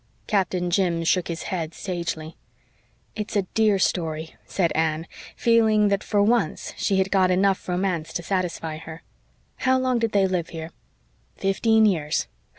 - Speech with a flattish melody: No, average, 3.7 semitones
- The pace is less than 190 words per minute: Yes, average, 155 wpm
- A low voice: No, medium, 185 Hz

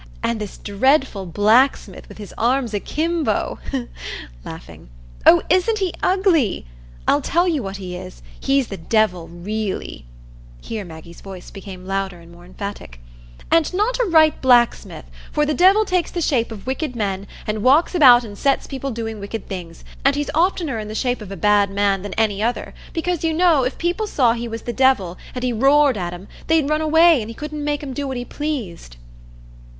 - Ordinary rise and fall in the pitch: No, wide, 7.3 semitones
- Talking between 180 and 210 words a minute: Yes, average, 185 wpm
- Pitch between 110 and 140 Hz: No, high, 235 Hz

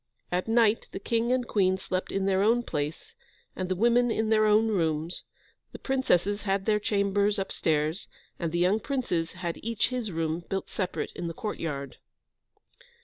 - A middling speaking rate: Yes, average, 170 wpm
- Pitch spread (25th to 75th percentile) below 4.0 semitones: No, average, 4.3 semitones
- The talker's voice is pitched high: Yes, high, 195 Hz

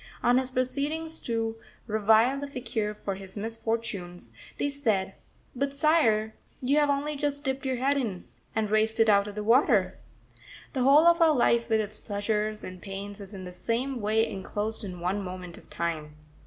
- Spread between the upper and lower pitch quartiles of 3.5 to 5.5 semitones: Yes, average, 4.7 semitones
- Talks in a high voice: Yes, high, 225 Hz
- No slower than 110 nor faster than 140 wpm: No, average, 180 wpm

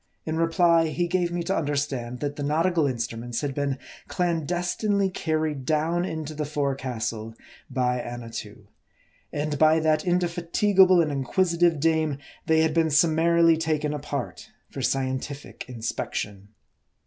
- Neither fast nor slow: No, slow, 130 wpm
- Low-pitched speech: No, medium, 155 Hz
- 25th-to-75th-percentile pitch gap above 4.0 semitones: No, average, 3.7 semitones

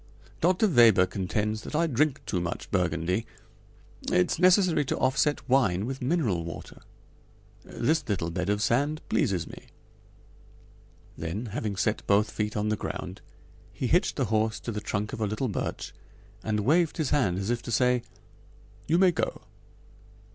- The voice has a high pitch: No, low, 110 Hz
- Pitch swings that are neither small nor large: No, wide, 6.5 semitones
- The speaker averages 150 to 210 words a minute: Yes, average, 160 wpm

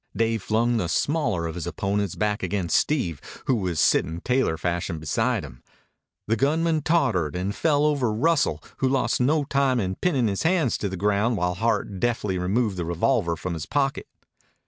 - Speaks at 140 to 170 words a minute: No, average, 180 wpm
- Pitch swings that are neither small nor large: No, wide, 6.9 semitones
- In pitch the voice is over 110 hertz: No, low, 105 Hz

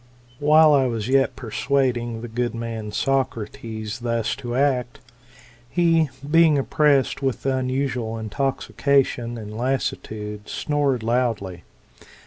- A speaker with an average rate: No, slow, 110 wpm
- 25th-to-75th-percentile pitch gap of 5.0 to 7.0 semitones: No, average, 3.3 semitones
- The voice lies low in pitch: Yes, low, 125 Hz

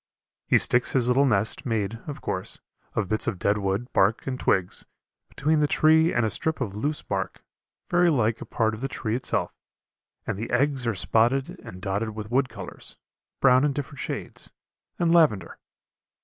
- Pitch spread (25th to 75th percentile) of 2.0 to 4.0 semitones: No, average, 4.7 semitones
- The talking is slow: No, average, 180 wpm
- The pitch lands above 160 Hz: No, low, 120 Hz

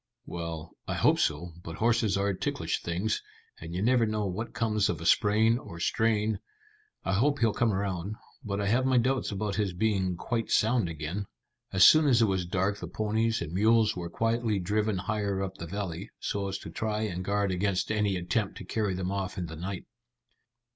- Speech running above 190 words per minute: Yes, average, 200 wpm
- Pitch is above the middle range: No, low, 100 Hz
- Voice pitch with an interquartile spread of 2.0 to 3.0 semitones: No, average, 3.4 semitones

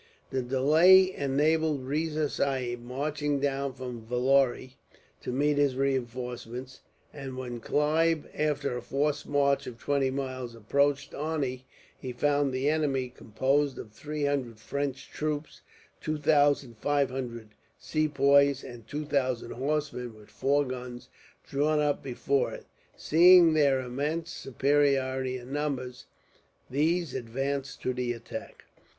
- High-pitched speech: No, medium, 140 Hz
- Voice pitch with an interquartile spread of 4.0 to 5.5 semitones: No, narrow, 2.5 semitones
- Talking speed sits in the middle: No, slow, 130 wpm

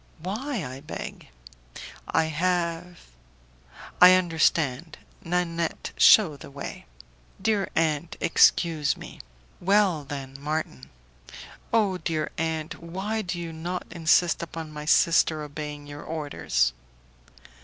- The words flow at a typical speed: No, slow, 110 wpm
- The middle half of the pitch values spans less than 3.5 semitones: Yes, average, 3.1 semitones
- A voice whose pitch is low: No, medium, 165 Hz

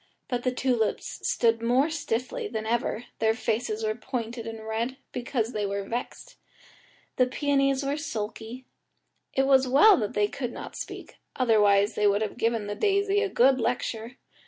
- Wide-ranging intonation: No, average, 3.3 semitones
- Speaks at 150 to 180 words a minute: Yes, average, 165 wpm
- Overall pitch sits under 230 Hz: No, high, 240 Hz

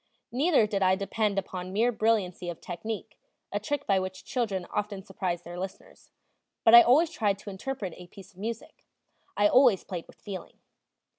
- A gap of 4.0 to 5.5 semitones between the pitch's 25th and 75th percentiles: No, average, 3.2 semitones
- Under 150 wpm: No, average, 175 wpm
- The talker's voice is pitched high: Yes, high, 200 Hz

